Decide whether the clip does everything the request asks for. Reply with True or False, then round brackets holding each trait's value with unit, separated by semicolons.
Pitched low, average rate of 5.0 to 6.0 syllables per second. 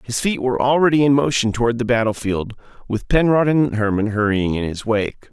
True (120 Hz; 5.6 syllables/s)